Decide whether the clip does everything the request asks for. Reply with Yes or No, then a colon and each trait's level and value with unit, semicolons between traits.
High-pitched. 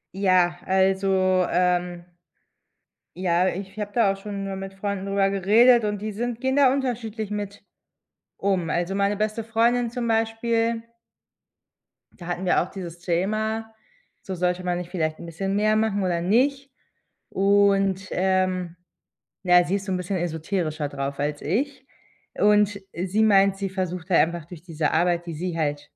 Yes: high, 195 Hz